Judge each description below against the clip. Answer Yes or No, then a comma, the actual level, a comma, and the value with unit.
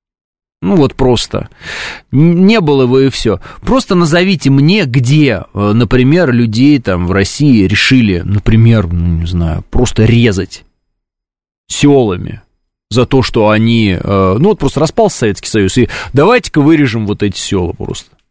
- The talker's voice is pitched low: Yes, low, 115 Hz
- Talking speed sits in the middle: Yes, average, 140 wpm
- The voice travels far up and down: Yes, wide, 6.3 semitones